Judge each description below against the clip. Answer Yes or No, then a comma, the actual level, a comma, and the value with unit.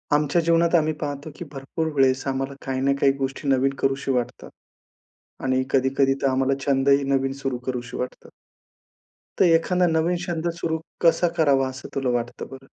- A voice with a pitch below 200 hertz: Yes, low, 135 Hz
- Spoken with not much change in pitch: No, average, 3.3 semitones